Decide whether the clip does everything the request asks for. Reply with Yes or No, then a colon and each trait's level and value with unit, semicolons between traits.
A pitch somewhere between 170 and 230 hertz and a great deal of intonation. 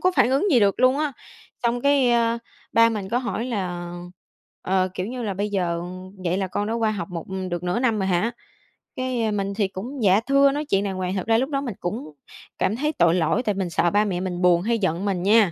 No: high, 205 Hz; average, 4.6 semitones